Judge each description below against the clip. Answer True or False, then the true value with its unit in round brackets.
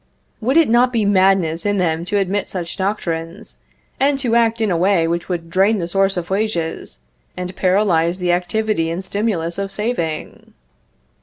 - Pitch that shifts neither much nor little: True (4.0 semitones)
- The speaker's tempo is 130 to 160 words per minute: False (170 wpm)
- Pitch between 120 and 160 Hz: False (190 Hz)